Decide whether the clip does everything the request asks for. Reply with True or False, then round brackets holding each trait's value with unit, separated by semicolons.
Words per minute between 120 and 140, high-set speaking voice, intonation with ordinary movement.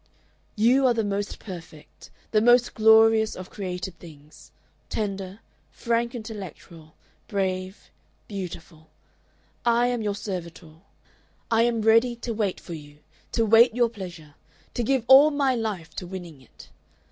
True (135 wpm; 210 Hz; 4.5 semitones)